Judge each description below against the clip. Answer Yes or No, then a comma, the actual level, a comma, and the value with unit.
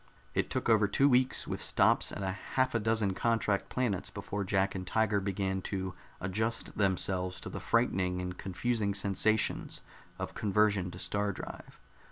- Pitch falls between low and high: No, low, 100 Hz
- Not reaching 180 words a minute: Yes, average, 160 wpm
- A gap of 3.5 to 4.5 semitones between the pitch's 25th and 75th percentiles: No, average, 2.7 semitones